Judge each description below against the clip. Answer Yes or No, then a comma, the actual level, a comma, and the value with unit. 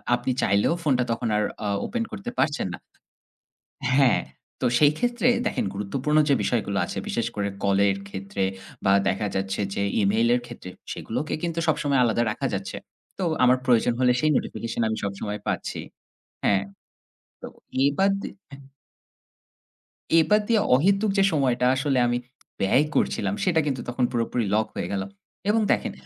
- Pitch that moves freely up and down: Yes, wide, 6.5 semitones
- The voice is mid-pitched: No, low, 125 Hz